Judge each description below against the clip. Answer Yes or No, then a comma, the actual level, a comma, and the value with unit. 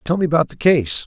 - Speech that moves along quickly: Yes, fast, 280 wpm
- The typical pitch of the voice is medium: Yes, medium, 150 Hz